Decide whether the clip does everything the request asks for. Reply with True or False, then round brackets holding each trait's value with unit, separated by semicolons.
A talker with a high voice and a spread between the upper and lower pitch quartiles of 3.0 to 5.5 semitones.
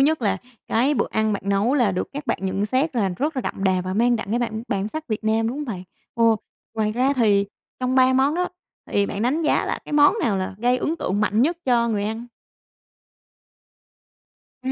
True (230 Hz; 4.3 semitones)